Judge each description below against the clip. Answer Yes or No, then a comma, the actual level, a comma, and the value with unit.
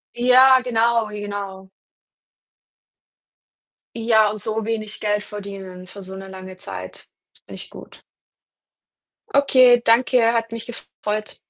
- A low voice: No, high, 215 Hz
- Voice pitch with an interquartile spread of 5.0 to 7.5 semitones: No, average, 2.8 semitones